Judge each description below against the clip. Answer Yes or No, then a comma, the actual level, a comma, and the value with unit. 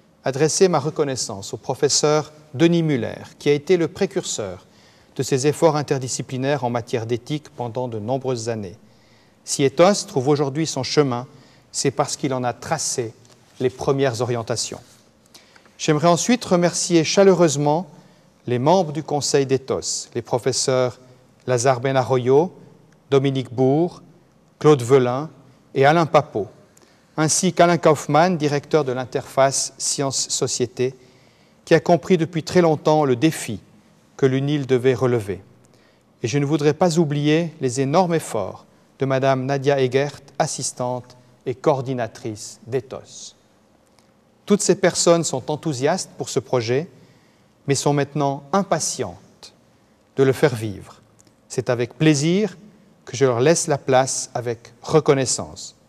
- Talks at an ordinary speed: No, slow, 130 wpm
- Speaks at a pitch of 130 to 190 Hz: Yes, medium, 140 Hz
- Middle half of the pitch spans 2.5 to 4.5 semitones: Yes, average, 3.8 semitones